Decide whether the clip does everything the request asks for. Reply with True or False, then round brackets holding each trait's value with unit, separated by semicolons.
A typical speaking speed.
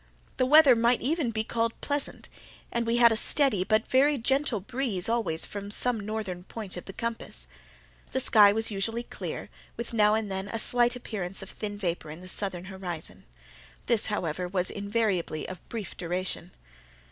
True (170 wpm)